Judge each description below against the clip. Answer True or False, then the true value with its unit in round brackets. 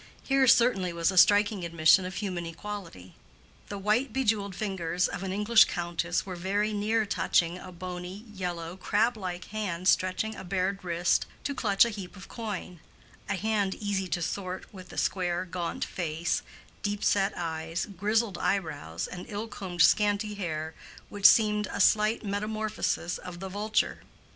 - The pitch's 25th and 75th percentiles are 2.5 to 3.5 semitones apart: True (2.9 semitones)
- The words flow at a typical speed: True (160 wpm)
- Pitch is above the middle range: True (195 Hz)